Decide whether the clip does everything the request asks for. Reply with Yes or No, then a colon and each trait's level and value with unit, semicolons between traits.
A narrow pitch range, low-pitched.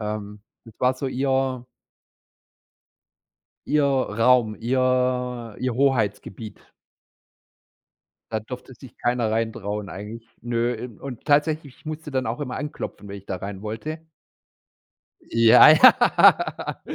No: average, 3.3 semitones; low, 120 Hz